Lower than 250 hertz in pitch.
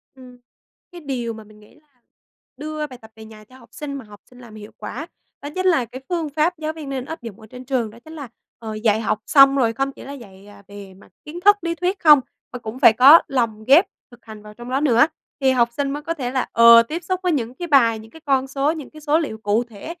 No: very high, 260 Hz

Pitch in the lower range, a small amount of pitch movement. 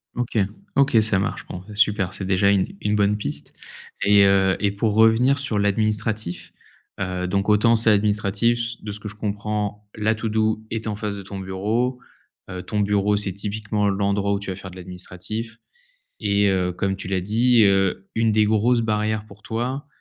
Yes: low, 105 Hz; narrow, 1.9 semitones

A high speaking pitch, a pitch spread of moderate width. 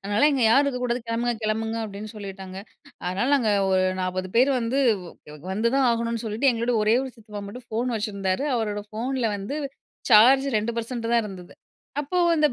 Yes: high, 230 Hz; average, 3.1 semitones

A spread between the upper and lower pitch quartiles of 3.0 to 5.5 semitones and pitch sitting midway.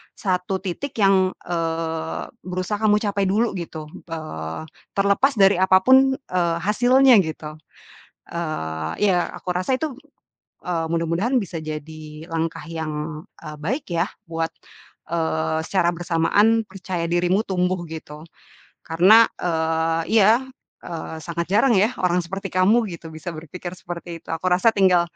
Yes: average, 3.4 semitones; medium, 175 Hz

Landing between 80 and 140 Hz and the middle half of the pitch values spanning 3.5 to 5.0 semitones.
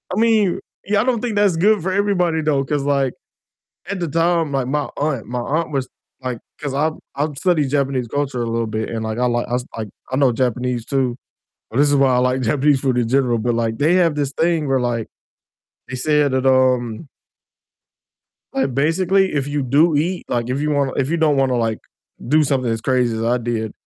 Yes: low, 135 Hz; average, 4.1 semitones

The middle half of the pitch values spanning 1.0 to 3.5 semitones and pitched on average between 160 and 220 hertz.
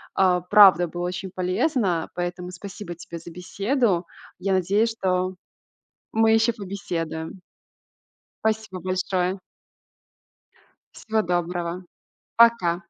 Yes: average, 2.8 semitones; medium, 185 Hz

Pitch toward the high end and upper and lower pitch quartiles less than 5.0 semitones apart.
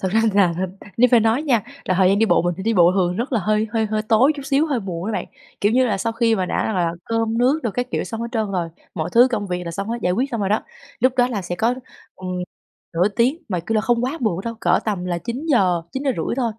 Yes: high, 220 Hz; average, 4.6 semitones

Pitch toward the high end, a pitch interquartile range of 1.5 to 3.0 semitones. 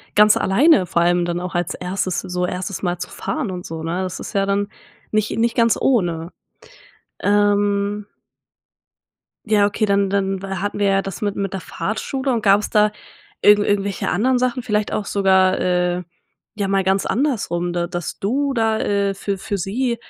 Yes: high, 200 Hz; narrow, 2.5 semitones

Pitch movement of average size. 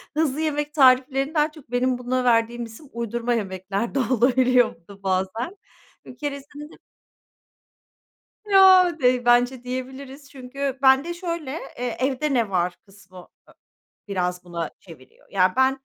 Yes: average, 4.0 semitones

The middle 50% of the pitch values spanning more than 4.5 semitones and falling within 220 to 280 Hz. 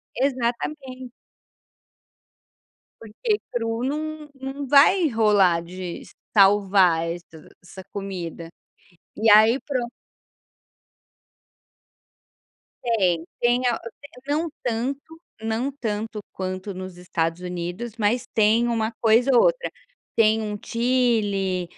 Yes: average, 5.1 semitones; high, 225 Hz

